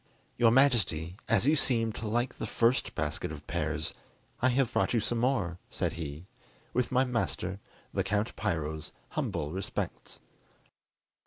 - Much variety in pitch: Yes, wide, 6.3 semitones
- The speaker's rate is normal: Yes, average, 150 wpm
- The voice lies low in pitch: Yes, low, 110 Hz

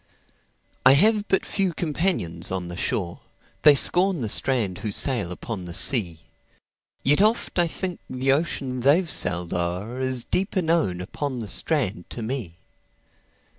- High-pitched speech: No, low, 130 Hz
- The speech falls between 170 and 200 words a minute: No, slow, 135 wpm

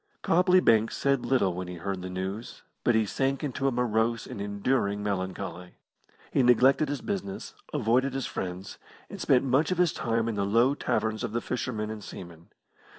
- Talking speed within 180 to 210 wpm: Yes, average, 185 wpm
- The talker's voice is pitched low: Yes, low, 115 Hz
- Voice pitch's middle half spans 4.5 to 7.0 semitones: Yes, average, 5.0 semitones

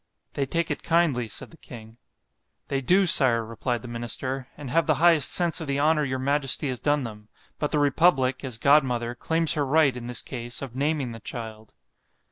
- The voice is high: No, low, 135 Hz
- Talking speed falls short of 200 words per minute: Yes, average, 190 wpm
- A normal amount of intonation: Yes, average, 4.0 semitones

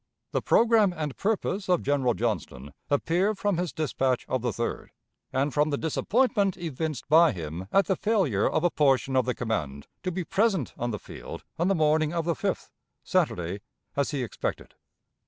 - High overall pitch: No, medium, 150 Hz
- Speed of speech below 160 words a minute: No, average, 180 wpm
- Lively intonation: Yes, wide, 6.7 semitones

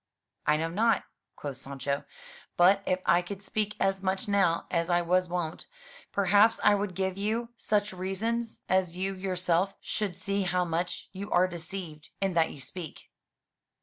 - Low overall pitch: No, medium, 185 Hz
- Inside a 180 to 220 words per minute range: No, average, 165 wpm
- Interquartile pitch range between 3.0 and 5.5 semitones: No, narrow, 2.5 semitones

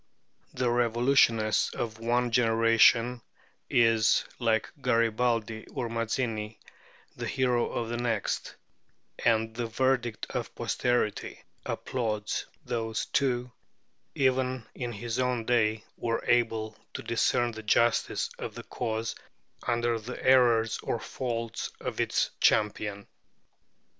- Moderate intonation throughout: No, narrow, 1.5 semitones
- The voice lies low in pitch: Yes, low, 115 Hz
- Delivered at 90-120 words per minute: Yes, slow, 115 wpm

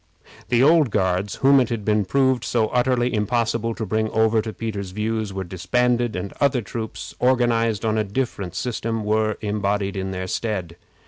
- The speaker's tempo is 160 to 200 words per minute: Yes, average, 175 wpm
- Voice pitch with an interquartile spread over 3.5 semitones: No, average, 3.1 semitones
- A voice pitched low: Yes, low, 110 Hz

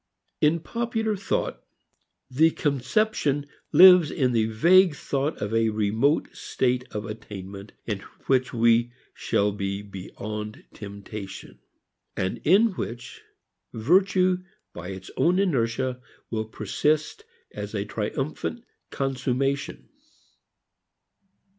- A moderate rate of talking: No, slow, 105 wpm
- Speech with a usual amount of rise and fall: No, wide, 7.3 semitones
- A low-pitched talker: Yes, low, 125 Hz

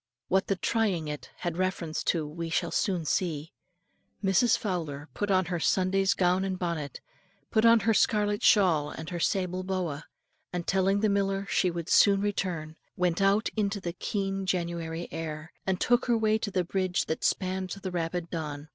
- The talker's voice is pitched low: No, medium, 185 Hz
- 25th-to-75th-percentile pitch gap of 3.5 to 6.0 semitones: No, average, 2.9 semitones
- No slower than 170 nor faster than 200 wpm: Yes, average, 180 wpm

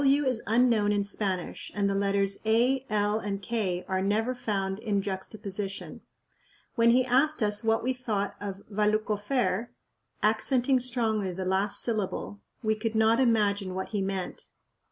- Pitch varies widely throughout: No, average, 2.9 semitones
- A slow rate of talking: No, average, 155 wpm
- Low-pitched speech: No, high, 210 Hz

